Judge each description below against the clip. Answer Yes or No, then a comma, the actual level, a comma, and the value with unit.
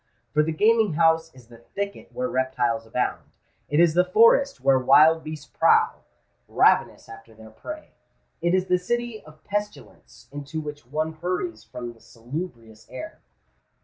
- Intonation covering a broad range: Yes, wide, 6.5 semitones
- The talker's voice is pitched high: No, medium, 155 Hz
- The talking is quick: No, average, 145 wpm